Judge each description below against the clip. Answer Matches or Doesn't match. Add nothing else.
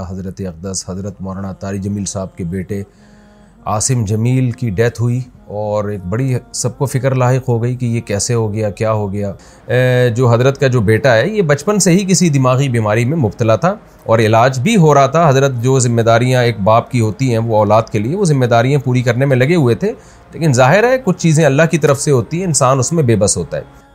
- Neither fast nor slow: Doesn't match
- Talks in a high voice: Doesn't match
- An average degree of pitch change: Matches